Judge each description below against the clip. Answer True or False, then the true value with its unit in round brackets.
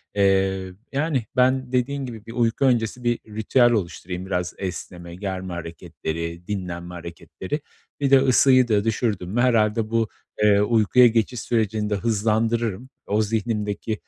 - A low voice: True (110 Hz)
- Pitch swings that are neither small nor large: True (4.0 semitones)